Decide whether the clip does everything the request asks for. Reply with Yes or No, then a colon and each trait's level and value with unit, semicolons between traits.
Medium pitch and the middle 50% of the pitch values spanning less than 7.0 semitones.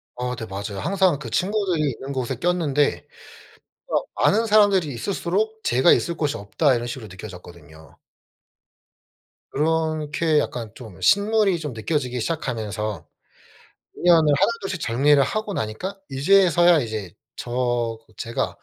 No: medium, 145 Hz; wide, 7.3 semitones